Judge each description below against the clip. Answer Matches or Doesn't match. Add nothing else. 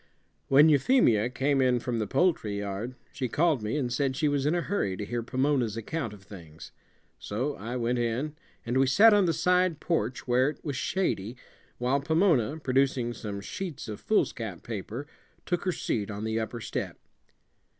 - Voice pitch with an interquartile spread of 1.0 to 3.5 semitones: Doesn't match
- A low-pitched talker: Matches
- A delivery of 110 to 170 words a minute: Doesn't match